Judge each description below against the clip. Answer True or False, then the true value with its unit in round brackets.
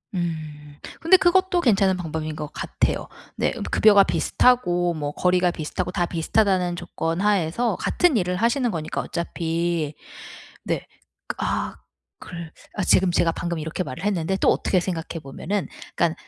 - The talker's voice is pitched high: False (175 Hz)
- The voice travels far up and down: False (3.4 semitones)